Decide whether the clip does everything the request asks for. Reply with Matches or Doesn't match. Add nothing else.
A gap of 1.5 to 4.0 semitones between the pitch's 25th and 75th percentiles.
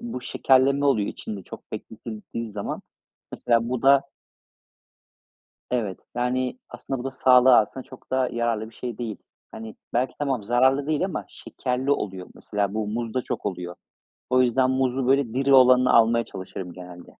Matches